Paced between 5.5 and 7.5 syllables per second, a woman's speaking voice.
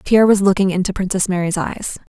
Yes: 6.4 syllables/s; female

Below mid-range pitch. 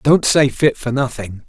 Yes: low, 130 Hz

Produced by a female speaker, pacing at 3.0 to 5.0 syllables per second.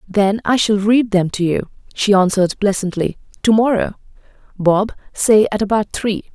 Yes: female; 4.8 syllables/s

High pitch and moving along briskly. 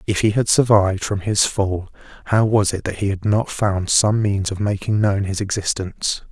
No: low, 100 Hz; fast, 210 wpm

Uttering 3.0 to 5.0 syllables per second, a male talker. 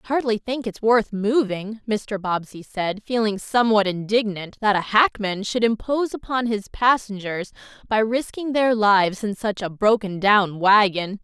No: 4.6 syllables/s; female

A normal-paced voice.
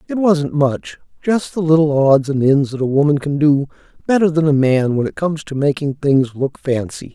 No: fast, 210 wpm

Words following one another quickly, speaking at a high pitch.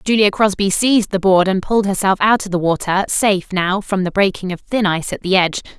Yes: fast, 240 wpm; high, 195 Hz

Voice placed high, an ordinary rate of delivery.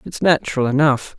No: medium, 140 Hz; average, 150 wpm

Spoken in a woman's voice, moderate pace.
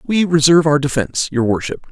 No: male; average, 190 wpm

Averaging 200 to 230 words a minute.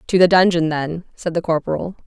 Yes: fast, 205 wpm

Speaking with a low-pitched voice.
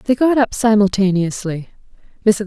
No: high, 210 Hz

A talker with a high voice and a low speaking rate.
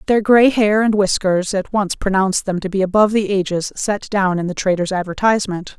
No: high, 195 Hz; fast, 205 wpm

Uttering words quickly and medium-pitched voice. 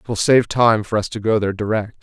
No: fast, 295 wpm; low, 110 Hz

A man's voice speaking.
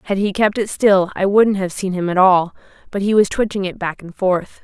No: female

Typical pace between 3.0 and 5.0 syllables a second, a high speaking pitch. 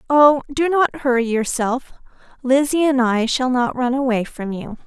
Yes: 4.5 syllables/s; very high, 260 Hz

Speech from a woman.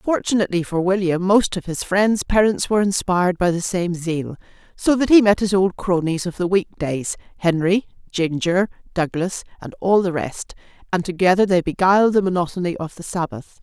Yes: female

